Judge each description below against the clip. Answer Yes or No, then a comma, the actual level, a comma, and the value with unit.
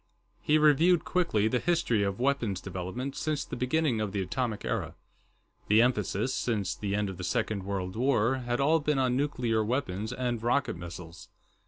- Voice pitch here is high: No, low, 120 Hz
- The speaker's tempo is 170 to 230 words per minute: Yes, average, 175 wpm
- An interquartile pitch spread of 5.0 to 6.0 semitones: Yes, wide, 5.4 semitones